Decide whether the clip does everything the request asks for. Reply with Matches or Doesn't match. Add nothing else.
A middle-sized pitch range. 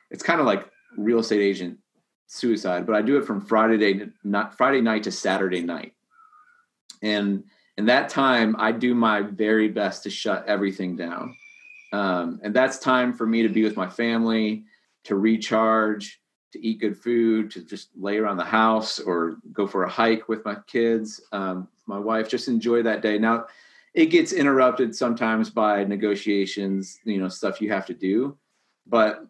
Doesn't match